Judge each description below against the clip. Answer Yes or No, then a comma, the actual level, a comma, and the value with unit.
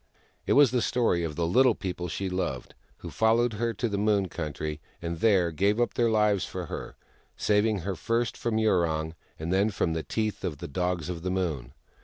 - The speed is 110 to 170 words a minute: No, fast, 205 wpm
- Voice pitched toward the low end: Yes, very low, 95 Hz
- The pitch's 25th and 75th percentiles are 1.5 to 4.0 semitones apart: No, average, 4.9 semitones